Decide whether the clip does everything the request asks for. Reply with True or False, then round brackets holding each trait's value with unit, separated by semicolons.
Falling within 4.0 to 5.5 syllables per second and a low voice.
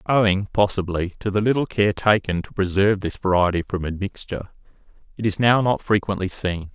False (5.7 syllables/s; 100 Hz)